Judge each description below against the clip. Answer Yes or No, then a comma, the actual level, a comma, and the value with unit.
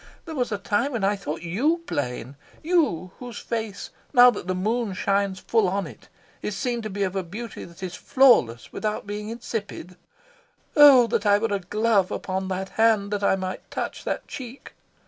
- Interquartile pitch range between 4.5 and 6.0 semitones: No, average, 3.9 semitones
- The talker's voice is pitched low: No, high, 205 Hz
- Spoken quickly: No, average, 190 wpm